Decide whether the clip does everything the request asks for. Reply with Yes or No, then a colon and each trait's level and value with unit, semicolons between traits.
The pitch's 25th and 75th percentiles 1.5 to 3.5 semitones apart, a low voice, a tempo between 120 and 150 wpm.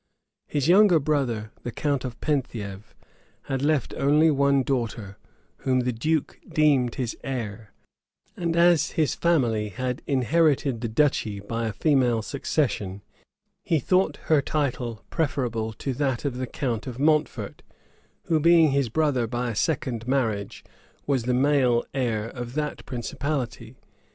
No: average, 4.2 semitones; low, 130 Hz; average, 140 wpm